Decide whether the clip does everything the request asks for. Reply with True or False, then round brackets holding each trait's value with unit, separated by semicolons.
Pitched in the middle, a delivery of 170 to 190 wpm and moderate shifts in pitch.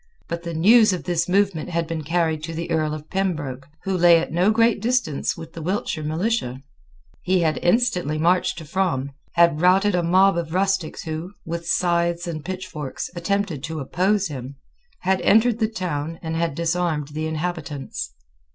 True (170 Hz; 175 wpm; 3.1 semitones)